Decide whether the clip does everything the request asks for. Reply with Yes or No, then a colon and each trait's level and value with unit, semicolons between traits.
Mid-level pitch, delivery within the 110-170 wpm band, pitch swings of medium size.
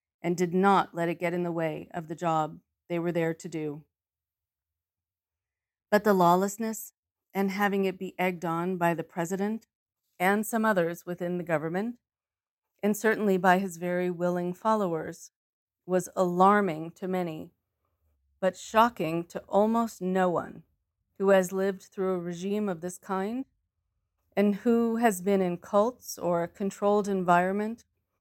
Yes: medium, 180 Hz; average, 150 wpm; average, 3.4 semitones